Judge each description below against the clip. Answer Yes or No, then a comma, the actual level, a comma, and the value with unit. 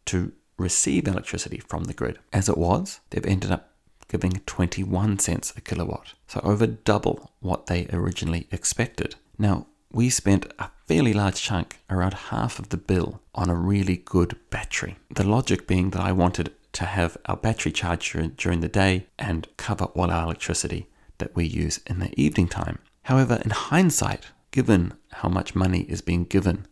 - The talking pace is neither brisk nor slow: Yes, average, 175 wpm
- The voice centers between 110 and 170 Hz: No, very low, 95 Hz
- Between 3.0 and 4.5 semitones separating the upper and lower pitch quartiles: Yes, average, 3.4 semitones